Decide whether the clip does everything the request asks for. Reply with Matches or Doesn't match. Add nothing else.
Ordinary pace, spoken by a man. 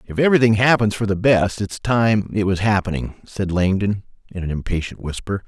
Matches